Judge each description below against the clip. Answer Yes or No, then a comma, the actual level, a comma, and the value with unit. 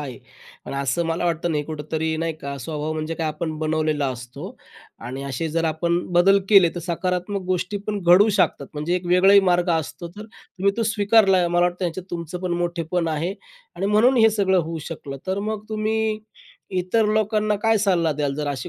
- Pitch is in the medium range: Yes, medium, 175 Hz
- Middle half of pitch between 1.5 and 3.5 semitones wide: No, average, 4.0 semitones